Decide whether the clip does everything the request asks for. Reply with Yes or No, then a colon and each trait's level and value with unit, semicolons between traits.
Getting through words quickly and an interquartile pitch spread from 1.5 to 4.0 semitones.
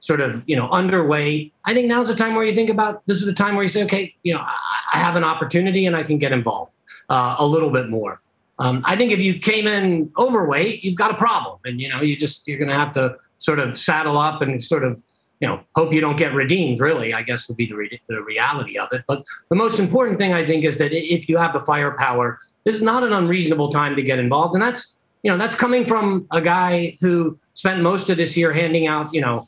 No: fast, 260 wpm; wide, 5.6 semitones